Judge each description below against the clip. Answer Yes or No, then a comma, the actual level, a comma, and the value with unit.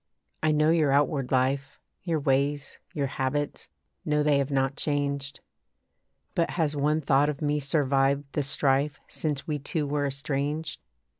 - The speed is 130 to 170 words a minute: Yes, average, 150 wpm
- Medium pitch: Yes, medium, 145 Hz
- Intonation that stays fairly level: Yes, narrow, 1.5 semitones